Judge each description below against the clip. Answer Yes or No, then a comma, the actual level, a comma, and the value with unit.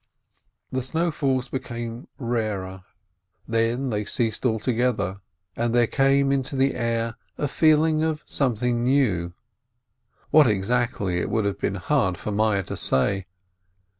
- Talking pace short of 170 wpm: Yes, average, 140 wpm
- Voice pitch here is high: No, low, 120 Hz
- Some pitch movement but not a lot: Yes, average, 4.4 semitones